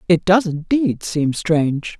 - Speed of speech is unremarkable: Yes, average, 150 wpm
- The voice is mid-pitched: Yes, medium, 175 Hz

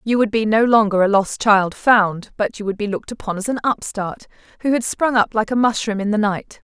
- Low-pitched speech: No, high, 215 Hz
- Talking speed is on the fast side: Yes, fast, 250 wpm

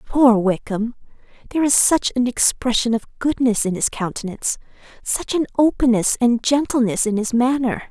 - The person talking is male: No, female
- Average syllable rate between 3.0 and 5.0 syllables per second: No, 5.2 syllables/s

